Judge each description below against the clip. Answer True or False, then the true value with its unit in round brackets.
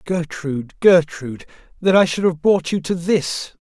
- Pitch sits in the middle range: True (170 Hz)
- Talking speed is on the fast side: False (150 wpm)